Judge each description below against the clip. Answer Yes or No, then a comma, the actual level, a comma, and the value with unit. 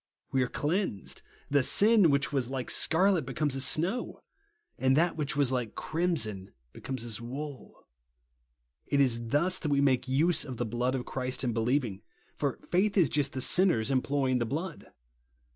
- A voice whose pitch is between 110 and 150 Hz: Yes, low, 135 Hz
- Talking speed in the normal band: Yes, average, 170 wpm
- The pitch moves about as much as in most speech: Yes, average, 4.2 semitones